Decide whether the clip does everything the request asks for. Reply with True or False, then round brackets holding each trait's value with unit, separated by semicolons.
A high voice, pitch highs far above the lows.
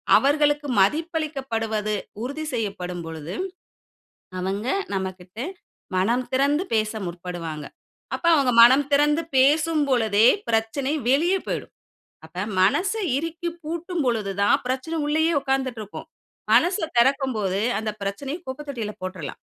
True (255 Hz; 6.7 semitones)